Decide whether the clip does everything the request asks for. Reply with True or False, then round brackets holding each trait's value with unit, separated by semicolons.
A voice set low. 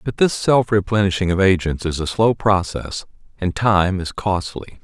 True (95 Hz)